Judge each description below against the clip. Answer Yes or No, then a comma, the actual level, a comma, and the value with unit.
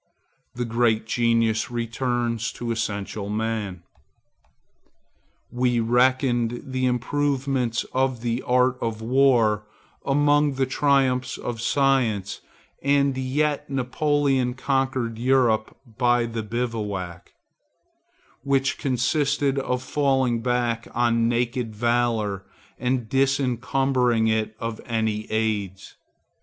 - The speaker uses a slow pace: Yes, slow, 100 wpm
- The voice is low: Yes, low, 120 Hz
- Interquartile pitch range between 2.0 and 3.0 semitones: Yes, average, 2.7 semitones